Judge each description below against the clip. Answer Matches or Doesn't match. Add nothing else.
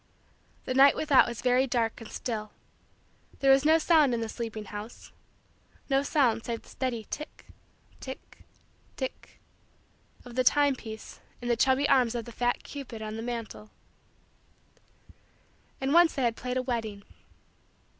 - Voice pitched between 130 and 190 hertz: Doesn't match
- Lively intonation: Doesn't match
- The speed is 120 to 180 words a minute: Matches